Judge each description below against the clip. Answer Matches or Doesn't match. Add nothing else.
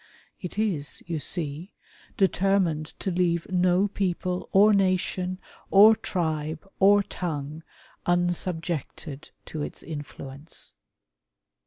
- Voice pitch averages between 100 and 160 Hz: Doesn't match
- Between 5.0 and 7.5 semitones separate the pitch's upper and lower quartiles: Doesn't match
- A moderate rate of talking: Doesn't match